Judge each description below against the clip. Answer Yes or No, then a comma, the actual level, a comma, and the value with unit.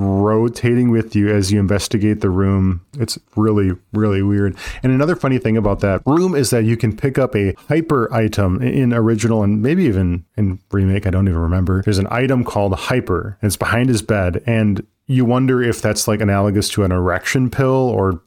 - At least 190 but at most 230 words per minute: Yes, average, 200 wpm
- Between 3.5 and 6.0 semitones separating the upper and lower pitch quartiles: Yes, average, 3.9 semitones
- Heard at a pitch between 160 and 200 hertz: No, low, 105 Hz